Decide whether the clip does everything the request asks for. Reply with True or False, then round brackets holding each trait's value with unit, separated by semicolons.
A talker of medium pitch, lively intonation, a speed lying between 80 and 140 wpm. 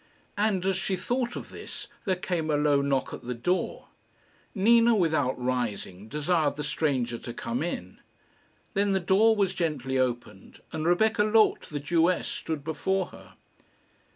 False (160 Hz; 6.4 semitones; 155 wpm)